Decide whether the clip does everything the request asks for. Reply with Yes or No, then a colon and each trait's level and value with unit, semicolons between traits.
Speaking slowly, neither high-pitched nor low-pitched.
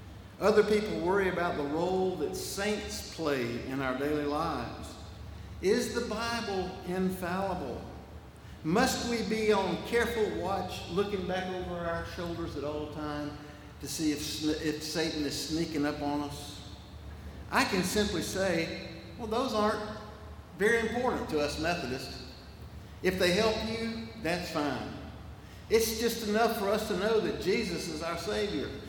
No: average, 145 wpm; medium, 175 Hz